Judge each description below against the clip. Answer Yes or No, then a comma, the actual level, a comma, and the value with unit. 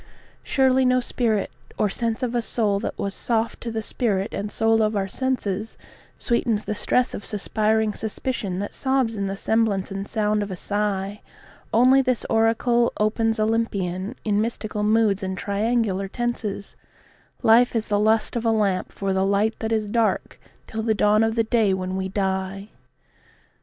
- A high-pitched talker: Yes, high, 215 Hz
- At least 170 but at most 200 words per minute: Yes, average, 175 wpm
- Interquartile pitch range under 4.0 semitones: Yes, narrow, 2.4 semitones